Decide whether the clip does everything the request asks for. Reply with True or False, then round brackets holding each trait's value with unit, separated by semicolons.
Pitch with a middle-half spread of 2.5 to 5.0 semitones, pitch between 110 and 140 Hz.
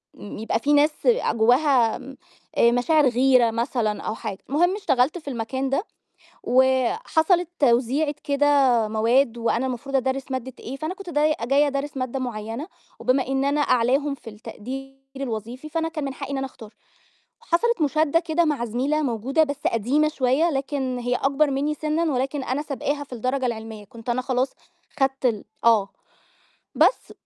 False (3.4 semitones; 270 Hz)